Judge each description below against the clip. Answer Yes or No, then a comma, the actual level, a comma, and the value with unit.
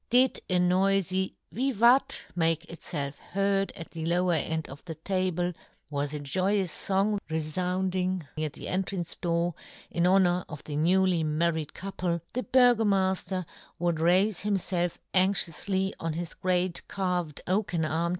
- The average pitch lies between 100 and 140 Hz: No, medium, 180 Hz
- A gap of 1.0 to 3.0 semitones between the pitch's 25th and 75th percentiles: Yes, average, 2.7 semitones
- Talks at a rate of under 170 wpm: Yes, average, 155 wpm